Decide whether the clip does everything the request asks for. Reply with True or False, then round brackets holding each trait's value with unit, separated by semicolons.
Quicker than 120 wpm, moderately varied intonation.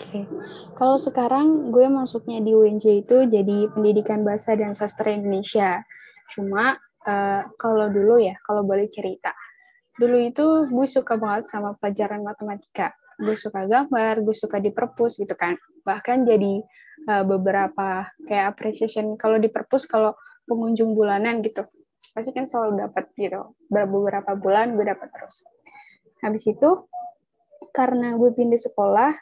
True (140 wpm; 3.4 semitones)